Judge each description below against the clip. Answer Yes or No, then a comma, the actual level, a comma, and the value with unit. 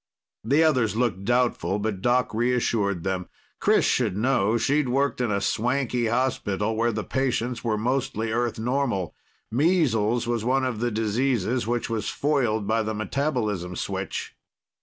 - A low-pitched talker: Yes, low, 115 Hz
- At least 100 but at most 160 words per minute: Yes, average, 150 wpm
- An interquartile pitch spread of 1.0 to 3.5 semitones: Yes, average, 3.0 semitones